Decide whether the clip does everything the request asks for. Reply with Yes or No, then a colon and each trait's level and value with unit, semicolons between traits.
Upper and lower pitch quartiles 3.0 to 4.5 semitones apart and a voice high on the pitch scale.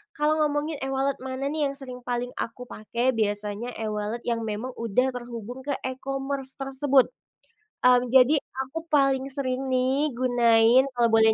No: narrow, 2.5 semitones; very high, 255 Hz